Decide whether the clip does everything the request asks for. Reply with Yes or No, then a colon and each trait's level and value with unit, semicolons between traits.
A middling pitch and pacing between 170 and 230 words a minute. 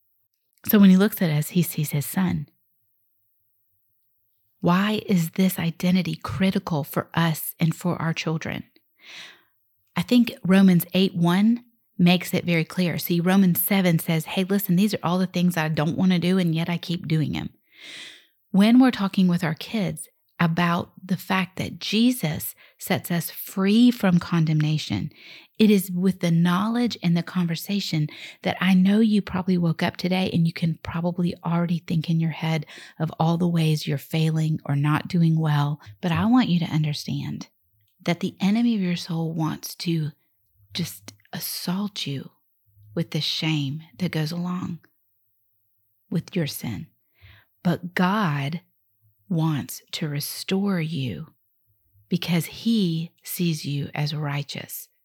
No: medium, 170 Hz; average, 155 wpm